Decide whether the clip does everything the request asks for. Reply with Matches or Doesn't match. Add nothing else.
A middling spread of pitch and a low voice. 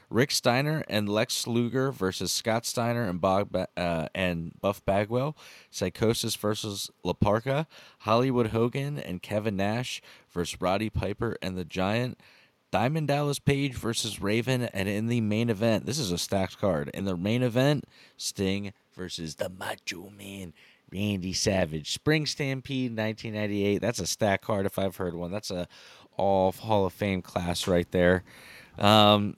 Matches